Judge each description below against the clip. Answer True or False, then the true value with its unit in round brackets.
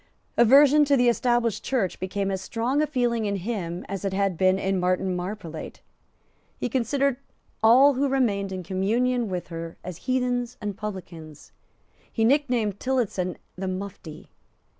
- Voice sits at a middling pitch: False (210 Hz)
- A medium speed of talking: True (150 wpm)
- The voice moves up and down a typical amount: True (5.0 semitones)